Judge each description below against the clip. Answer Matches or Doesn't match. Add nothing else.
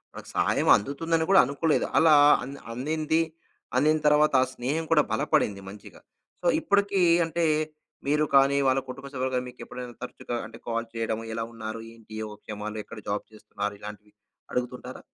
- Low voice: Matches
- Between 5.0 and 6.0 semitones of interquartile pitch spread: Matches